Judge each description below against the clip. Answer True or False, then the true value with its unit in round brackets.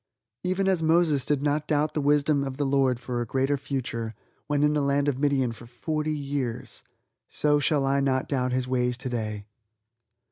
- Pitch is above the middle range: False (140 Hz)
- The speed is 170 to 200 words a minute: True (185 wpm)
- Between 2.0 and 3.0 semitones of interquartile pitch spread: True (2.6 semitones)